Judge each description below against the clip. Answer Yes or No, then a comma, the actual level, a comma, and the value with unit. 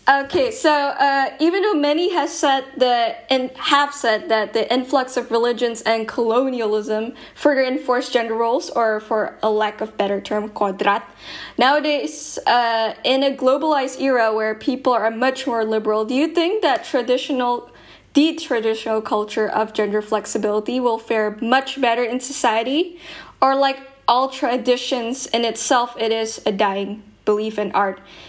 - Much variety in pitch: No, average, 3.9 semitones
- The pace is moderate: No, fast, 155 wpm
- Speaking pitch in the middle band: No, high, 245 Hz